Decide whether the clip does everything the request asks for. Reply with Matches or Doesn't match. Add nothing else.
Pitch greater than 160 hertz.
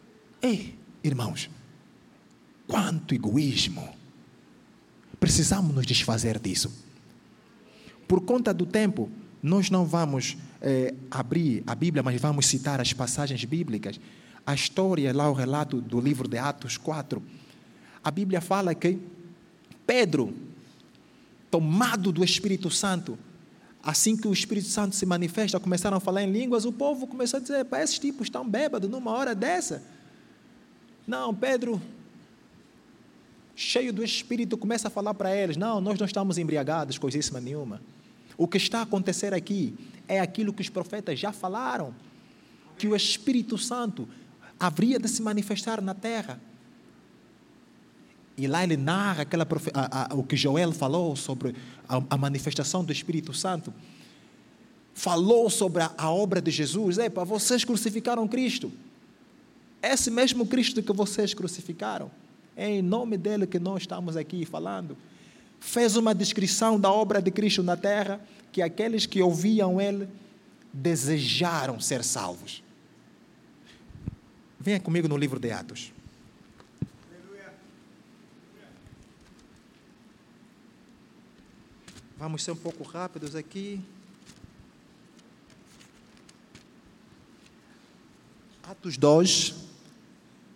Matches